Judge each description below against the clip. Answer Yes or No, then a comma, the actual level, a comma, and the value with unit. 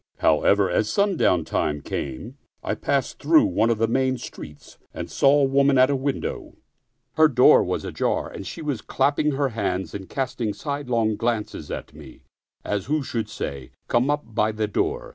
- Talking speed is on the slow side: No, average, 185 wpm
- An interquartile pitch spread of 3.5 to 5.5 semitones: Yes, average, 4.9 semitones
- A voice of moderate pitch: No, low, 130 Hz